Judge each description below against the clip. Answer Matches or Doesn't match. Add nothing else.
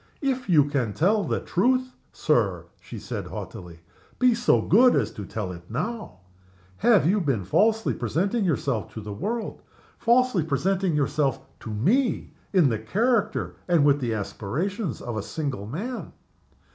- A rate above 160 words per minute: Doesn't match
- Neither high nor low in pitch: Matches